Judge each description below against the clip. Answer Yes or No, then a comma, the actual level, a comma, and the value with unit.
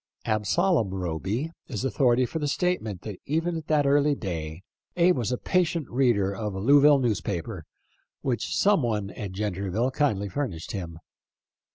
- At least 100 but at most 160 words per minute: Yes, average, 155 wpm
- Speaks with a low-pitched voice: Yes, low, 120 Hz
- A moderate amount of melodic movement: No, wide, 6.8 semitones